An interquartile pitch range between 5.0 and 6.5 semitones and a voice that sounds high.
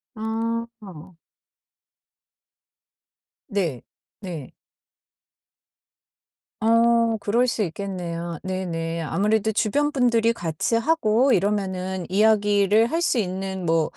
No: average, 4.0 semitones; high, 205 Hz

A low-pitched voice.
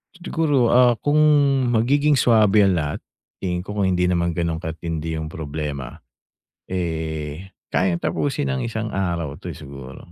Yes: very low, 90 Hz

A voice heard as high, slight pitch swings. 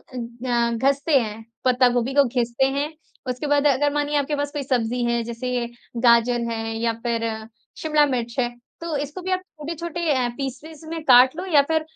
No: very high, 260 Hz; average, 3.6 semitones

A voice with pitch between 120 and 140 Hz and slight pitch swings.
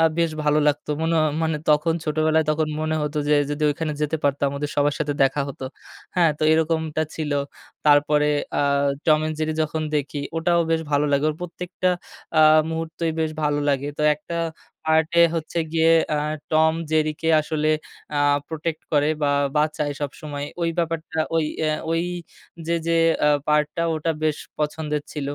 No: medium, 155 Hz; narrow, 1.5 semitones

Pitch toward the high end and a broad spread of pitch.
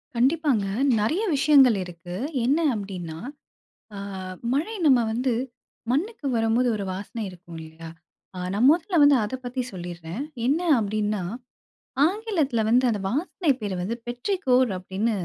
Yes: high, 235 Hz; wide, 6.4 semitones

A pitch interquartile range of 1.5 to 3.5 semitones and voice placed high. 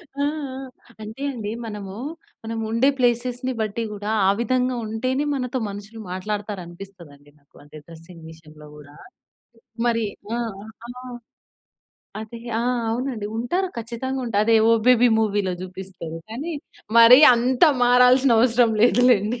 No: average, 4.0 semitones; high, 225 Hz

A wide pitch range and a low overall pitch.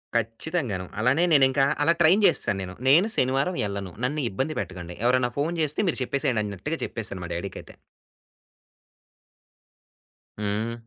Yes: wide, 7.0 semitones; low, 125 Hz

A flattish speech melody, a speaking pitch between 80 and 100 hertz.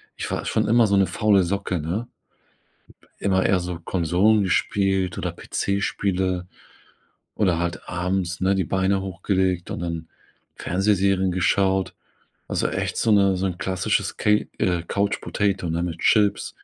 Yes: narrow, 1.9 semitones; very low, 95 Hz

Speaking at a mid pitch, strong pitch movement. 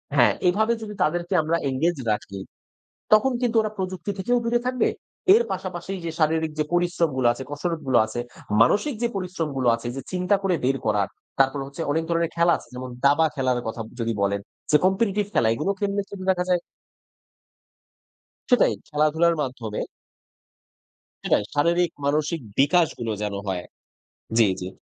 Yes: medium, 160 Hz; wide, 6.1 semitones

